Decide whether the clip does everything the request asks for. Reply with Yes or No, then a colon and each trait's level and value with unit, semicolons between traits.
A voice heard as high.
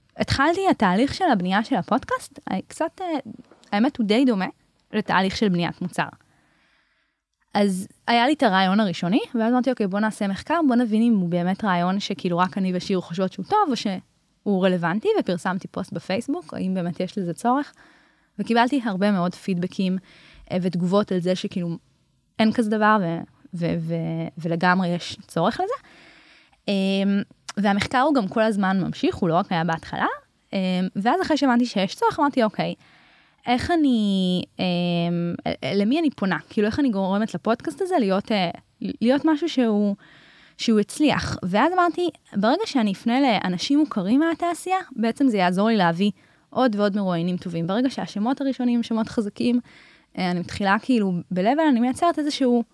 Yes: high, 205 Hz